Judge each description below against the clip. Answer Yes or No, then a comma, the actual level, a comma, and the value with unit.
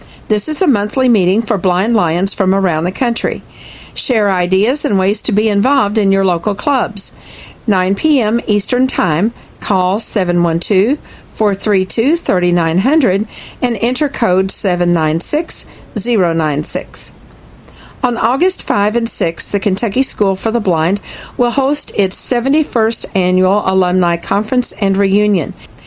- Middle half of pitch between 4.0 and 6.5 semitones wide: Yes, average, 4.3 semitones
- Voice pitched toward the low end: No, high, 205 Hz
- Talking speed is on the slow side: Yes, slow, 130 wpm